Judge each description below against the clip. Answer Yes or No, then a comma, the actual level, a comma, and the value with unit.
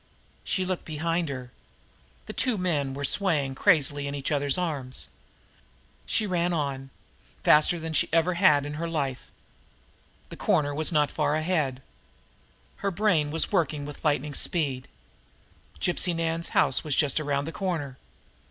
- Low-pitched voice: No, medium, 150 Hz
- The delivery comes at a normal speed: Yes, average, 155 wpm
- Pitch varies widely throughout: No, average, 3.1 semitones